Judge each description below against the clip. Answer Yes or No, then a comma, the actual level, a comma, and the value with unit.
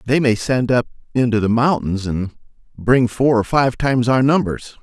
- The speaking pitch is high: No, low, 120 Hz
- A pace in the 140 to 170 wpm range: No, average, 185 wpm